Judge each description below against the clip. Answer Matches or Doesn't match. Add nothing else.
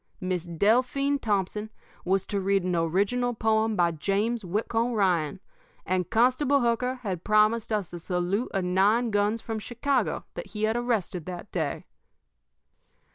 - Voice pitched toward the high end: Matches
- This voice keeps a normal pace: Matches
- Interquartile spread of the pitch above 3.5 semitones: Matches